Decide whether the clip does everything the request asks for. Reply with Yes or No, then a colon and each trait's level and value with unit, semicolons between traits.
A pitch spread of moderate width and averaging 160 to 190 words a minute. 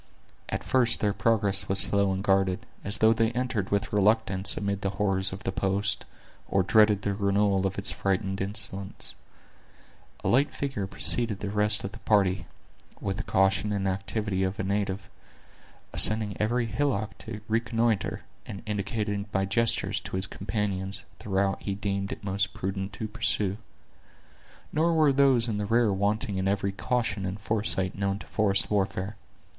No: narrow, 2.1 semitones; average, 165 wpm